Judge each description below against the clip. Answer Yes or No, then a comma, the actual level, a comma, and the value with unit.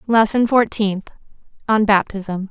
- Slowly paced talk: Yes, slow, 95 wpm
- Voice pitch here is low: No, high, 210 Hz